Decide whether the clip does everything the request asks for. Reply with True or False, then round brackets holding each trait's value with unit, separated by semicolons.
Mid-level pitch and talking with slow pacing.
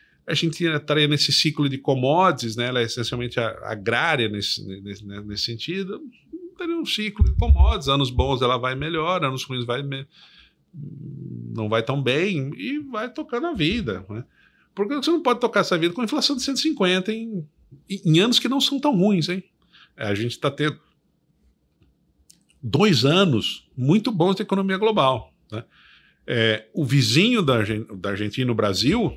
False (145 Hz; 165 wpm)